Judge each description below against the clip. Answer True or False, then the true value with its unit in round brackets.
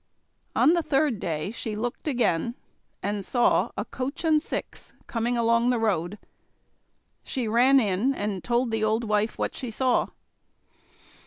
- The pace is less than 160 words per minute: True (150 wpm)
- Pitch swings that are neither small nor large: True (3.3 semitones)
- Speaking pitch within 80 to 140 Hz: False (235 Hz)